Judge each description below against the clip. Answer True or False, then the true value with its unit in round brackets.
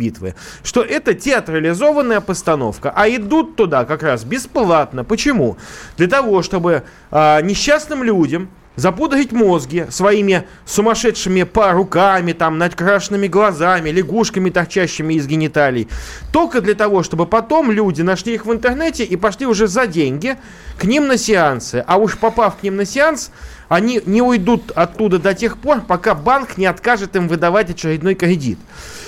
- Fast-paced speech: False (145 wpm)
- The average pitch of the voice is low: False (200 Hz)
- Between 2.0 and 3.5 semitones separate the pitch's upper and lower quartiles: False (4.9 semitones)